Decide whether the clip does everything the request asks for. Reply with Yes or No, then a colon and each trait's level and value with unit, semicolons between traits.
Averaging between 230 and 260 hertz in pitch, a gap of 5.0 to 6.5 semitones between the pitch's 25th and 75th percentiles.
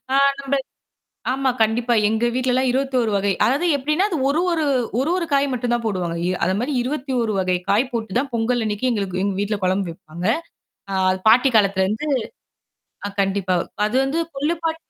Yes: high, 240 Hz; average, 5.3 semitones